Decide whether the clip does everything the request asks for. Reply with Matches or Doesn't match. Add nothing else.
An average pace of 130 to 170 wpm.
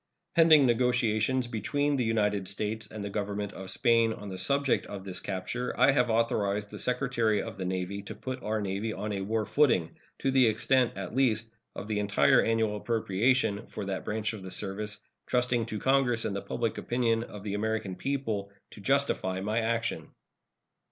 Doesn't match